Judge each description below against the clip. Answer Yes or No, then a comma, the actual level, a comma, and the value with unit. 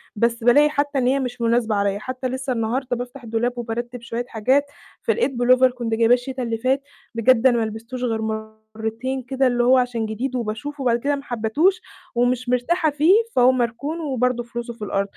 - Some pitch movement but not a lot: No, narrow, 2.2 semitones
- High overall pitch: Yes, high, 245 Hz